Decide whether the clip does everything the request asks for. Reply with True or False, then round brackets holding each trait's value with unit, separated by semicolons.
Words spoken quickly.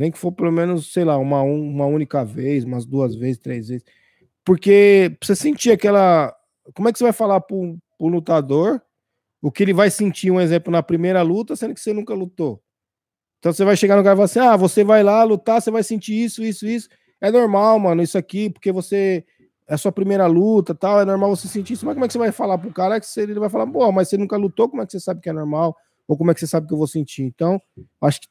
True (265 wpm)